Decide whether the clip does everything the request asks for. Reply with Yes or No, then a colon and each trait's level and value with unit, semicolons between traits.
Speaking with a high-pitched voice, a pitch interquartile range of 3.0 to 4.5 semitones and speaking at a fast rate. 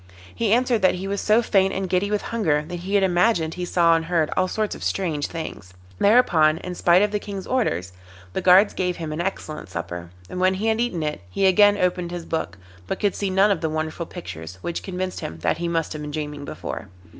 No: medium, 180 Hz; average, 4.0 semitones; fast, 235 wpm